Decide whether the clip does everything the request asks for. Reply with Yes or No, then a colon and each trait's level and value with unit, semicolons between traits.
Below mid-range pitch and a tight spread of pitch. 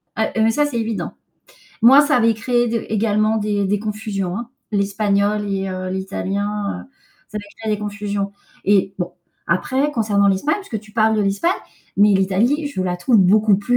No: high, 210 Hz; narrow, 2.2 semitones